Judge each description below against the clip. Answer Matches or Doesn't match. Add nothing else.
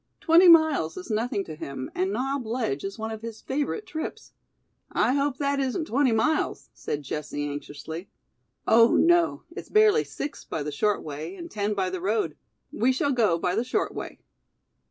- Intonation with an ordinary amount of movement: Doesn't match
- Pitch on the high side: Matches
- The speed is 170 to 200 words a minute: Matches